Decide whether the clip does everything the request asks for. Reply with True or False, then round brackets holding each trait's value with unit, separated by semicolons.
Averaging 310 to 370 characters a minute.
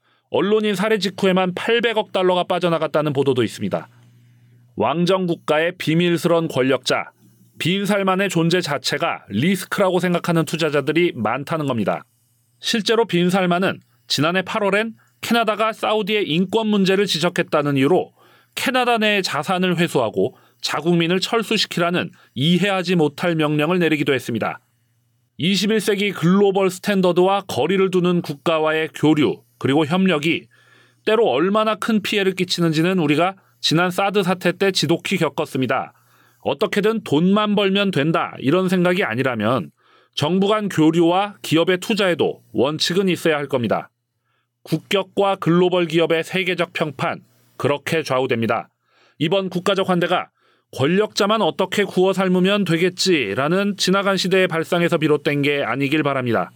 True (330 characters per minute)